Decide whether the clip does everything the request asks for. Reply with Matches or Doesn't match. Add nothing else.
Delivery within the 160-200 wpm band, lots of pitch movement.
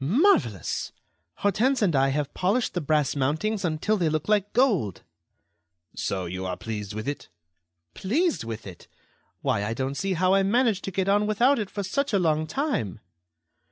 Matches